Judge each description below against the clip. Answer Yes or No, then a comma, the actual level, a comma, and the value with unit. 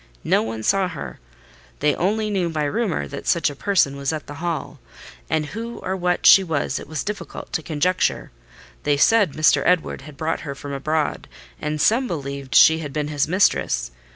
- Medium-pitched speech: Yes, medium, 155 Hz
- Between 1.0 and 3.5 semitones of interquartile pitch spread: No, average, 4.3 semitones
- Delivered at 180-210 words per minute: Yes, average, 190 wpm